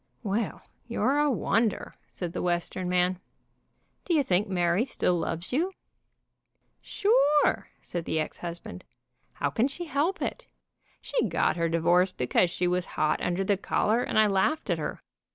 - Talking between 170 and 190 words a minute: No, average, 160 wpm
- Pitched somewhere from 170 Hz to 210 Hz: Yes, high, 190 Hz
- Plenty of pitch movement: Yes, wide, 6.5 semitones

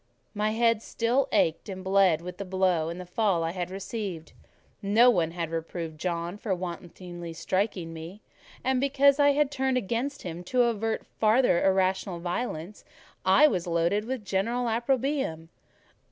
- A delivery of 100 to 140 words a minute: No, average, 155 wpm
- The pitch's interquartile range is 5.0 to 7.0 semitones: Yes, wide, 5.4 semitones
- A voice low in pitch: No, high, 195 Hz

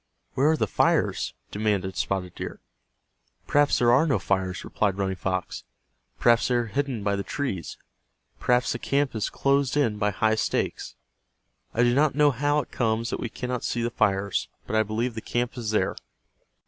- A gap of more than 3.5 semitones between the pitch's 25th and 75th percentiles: Yes, average, 4.4 semitones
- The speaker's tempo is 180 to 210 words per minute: Yes, average, 185 wpm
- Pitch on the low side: Yes, low, 115 Hz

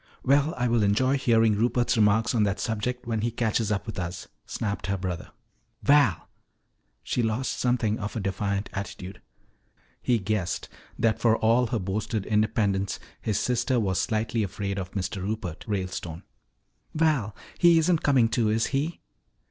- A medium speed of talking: Yes, average, 155 wpm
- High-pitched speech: No, low, 110 Hz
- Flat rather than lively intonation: No, average, 3.4 semitones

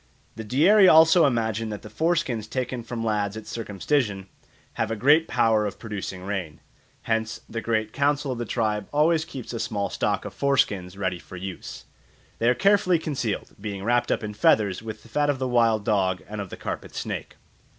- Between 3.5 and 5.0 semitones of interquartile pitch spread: Yes, average, 4.6 semitones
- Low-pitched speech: Yes, low, 115 Hz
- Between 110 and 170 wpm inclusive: No, average, 190 wpm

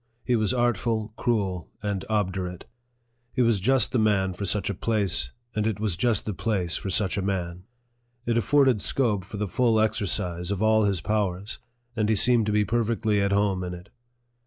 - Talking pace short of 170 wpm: No, average, 190 wpm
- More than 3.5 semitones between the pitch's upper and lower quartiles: No, average, 2.8 semitones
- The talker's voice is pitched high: No, low, 105 Hz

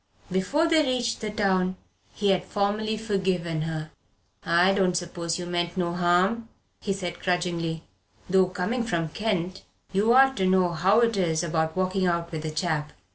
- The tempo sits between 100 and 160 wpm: No, average, 170 wpm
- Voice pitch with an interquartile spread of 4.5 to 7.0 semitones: No, average, 3.0 semitones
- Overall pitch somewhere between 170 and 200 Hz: Yes, medium, 185 Hz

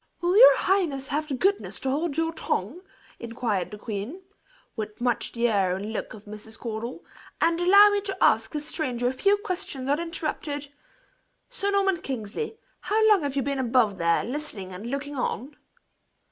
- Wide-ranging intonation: Yes, wide, 7.6 semitones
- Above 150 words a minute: Yes, average, 175 wpm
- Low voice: No, very high, 275 Hz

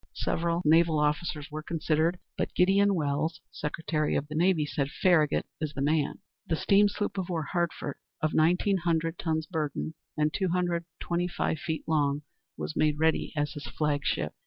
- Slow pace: No, average, 175 wpm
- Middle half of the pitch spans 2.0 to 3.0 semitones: Yes, narrow, 2.4 semitones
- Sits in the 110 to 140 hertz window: No, medium, 160 Hz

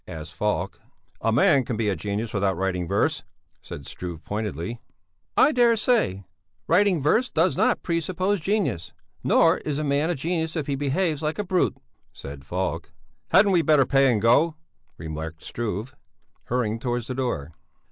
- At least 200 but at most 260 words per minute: No, average, 165 wpm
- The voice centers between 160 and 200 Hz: No, low, 130 Hz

